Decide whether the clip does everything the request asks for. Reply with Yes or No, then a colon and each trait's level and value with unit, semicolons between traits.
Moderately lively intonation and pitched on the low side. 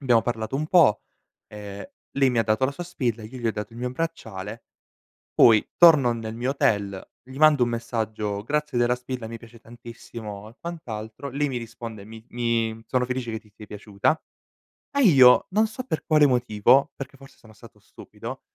Yes: average, 3.7 semitones; low, 120 Hz